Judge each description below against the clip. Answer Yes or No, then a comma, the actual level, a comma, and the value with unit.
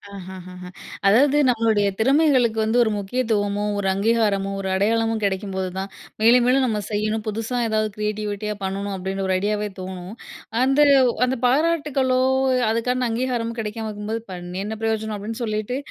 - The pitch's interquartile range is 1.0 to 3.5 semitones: Yes, average, 2.9 semitones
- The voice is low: No, high, 215 Hz